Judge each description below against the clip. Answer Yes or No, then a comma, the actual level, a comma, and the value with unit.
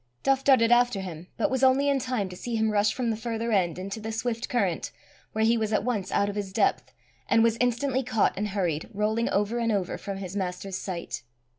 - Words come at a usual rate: No, fast, 230 wpm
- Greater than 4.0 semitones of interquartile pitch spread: No, average, 3.4 semitones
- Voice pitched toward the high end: Yes, high, 220 Hz